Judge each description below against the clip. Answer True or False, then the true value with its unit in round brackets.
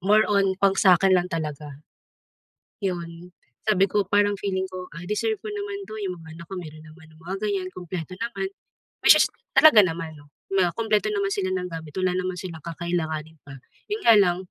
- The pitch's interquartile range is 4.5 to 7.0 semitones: False (3.3 semitones)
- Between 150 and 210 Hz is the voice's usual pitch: True (185 Hz)